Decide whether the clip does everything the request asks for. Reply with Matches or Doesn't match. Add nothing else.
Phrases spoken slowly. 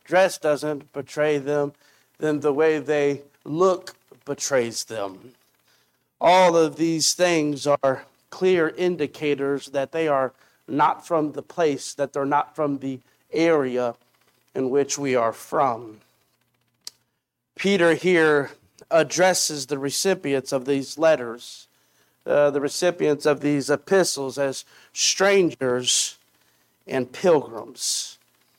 Matches